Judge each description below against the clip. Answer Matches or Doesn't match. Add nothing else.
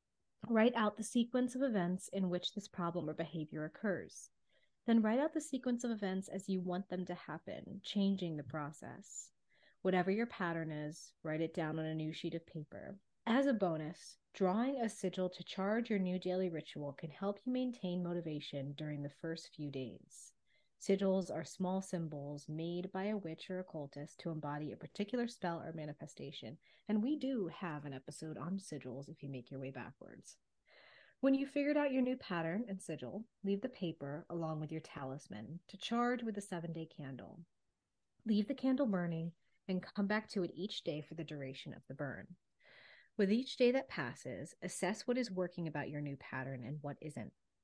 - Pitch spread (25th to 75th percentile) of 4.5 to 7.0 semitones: Matches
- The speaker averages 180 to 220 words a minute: Matches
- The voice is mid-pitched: Matches